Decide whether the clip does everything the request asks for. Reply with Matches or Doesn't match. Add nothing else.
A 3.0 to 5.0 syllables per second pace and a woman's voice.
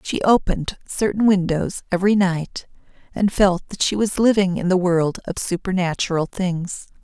Matches